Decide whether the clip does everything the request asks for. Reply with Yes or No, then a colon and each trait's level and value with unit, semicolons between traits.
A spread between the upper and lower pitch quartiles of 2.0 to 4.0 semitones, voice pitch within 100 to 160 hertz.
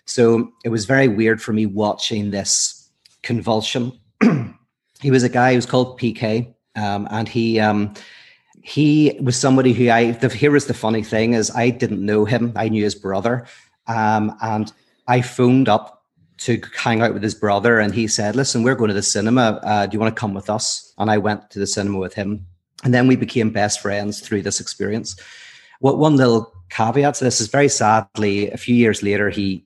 Yes: average, 2.8 semitones; low, 110 Hz